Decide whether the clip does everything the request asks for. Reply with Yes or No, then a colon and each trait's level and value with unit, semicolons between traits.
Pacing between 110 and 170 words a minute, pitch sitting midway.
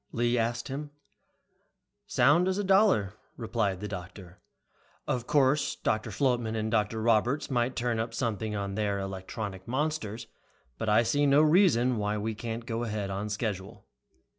No: average, 155 wpm; low, 115 Hz